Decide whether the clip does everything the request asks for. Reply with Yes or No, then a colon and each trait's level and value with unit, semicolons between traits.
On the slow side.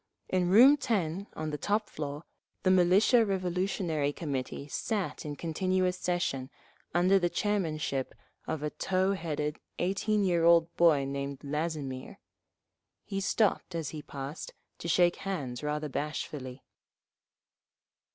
Yes: slow, 125 wpm